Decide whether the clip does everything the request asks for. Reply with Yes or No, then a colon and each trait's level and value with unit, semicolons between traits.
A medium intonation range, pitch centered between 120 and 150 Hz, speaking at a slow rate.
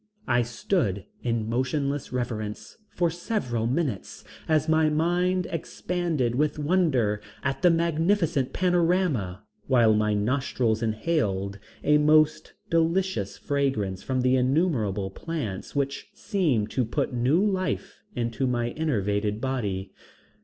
No: wide, 6.7 semitones; low, 135 Hz; slow, 115 wpm